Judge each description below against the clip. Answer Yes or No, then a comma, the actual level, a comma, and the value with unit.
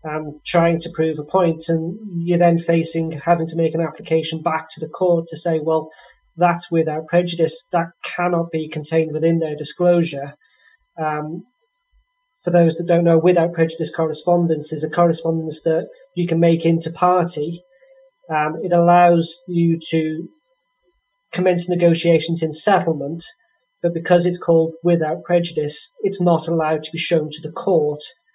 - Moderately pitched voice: Yes, medium, 165 Hz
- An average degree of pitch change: No, narrow, 1.6 semitones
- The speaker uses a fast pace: No, average, 160 wpm